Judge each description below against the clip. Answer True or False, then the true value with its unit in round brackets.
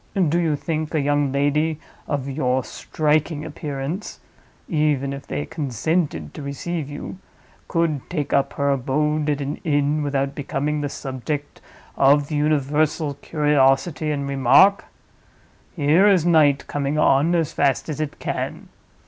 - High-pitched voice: False (145 Hz)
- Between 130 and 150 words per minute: True (140 wpm)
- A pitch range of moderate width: False (2.0 semitones)